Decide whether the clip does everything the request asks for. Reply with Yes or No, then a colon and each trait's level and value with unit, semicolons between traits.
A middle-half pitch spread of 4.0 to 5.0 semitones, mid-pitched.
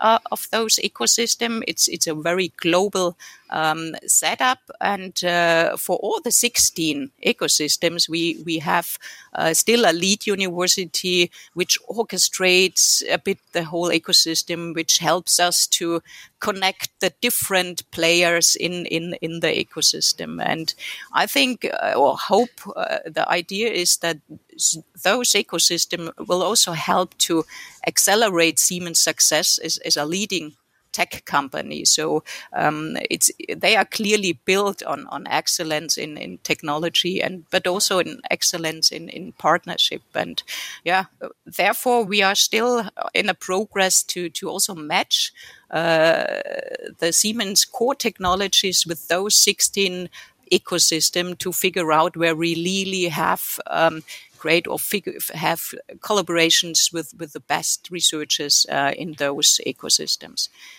No: average, 3.3 semitones; medium, 175 Hz